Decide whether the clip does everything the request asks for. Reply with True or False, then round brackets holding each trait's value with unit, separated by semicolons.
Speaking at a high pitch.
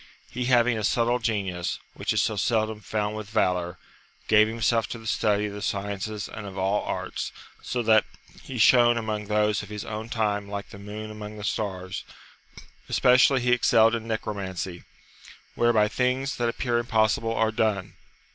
False (110 Hz)